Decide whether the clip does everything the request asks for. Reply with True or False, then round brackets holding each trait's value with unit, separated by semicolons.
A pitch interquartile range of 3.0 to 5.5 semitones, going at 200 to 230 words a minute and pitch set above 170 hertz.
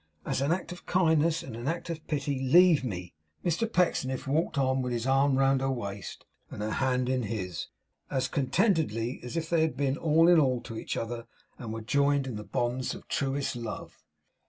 False (4.8 semitones; 205 wpm; 135 Hz)